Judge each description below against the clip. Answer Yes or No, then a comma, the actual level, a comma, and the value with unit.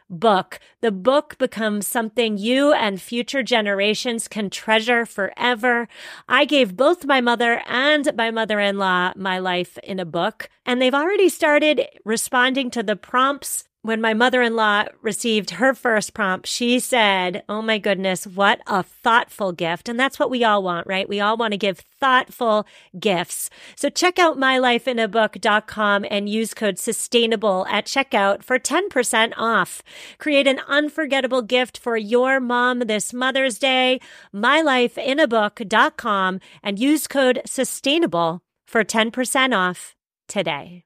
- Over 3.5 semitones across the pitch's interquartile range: Yes, average, 4.2 semitones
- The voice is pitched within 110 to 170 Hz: No, high, 230 Hz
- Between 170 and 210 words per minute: No, average, 140 wpm